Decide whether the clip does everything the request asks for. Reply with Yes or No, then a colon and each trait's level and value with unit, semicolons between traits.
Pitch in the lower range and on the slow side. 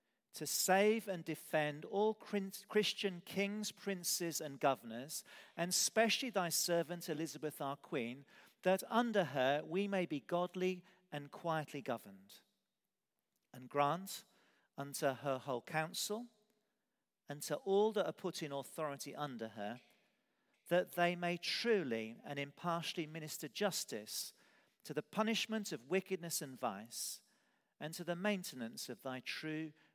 No: medium, 170 Hz; slow, 130 wpm